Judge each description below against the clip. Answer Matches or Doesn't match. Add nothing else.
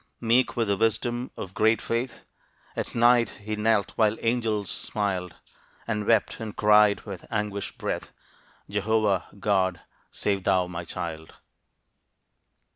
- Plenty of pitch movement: Doesn't match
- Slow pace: Matches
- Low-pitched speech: Matches